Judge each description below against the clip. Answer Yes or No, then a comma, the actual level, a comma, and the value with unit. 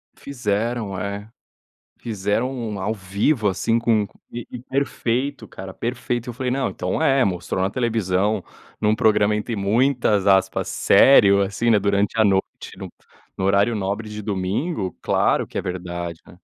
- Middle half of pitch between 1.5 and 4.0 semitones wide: Yes, average, 3.3 semitones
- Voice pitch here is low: Yes, low, 105 Hz